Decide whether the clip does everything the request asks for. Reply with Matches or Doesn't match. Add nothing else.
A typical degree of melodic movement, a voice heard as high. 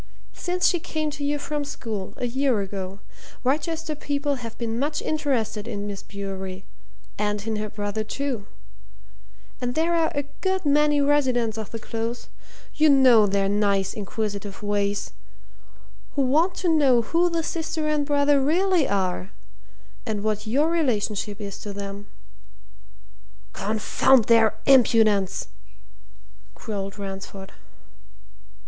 Doesn't match